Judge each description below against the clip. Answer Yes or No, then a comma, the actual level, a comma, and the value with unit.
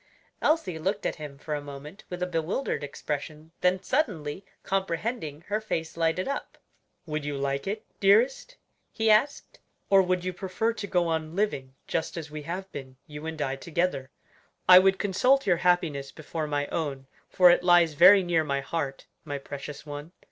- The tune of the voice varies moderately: Yes, average, 4.5 semitones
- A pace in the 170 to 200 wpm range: Yes, average, 175 wpm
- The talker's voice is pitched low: No, medium, 165 Hz